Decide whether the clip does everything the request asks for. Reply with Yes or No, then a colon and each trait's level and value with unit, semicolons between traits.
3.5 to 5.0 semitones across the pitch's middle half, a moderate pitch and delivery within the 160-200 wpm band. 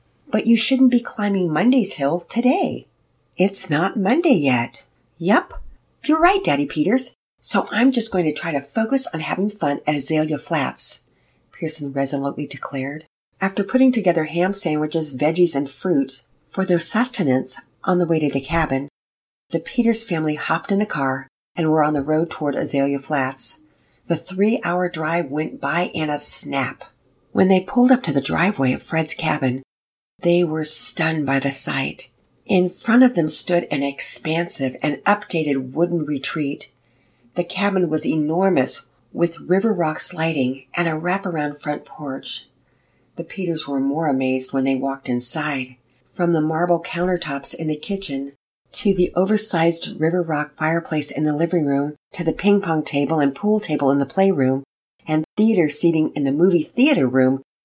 Yes: average, 4.6 semitones; medium, 160 Hz; average, 165 wpm